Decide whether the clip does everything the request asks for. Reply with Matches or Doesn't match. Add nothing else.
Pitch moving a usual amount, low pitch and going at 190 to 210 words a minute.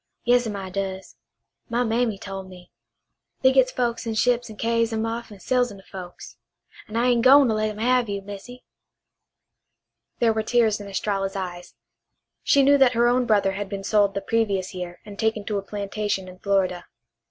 Doesn't match